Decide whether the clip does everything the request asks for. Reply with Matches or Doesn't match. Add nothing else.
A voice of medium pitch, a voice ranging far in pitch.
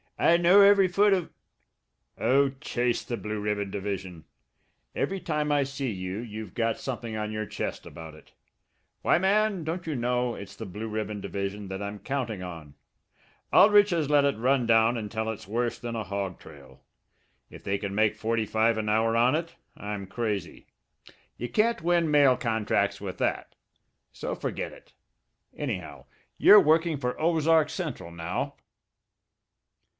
Doesn't match